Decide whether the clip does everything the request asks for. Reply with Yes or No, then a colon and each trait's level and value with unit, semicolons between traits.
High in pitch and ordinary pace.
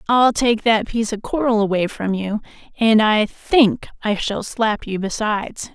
Yes: high, 220 Hz; average, 180 wpm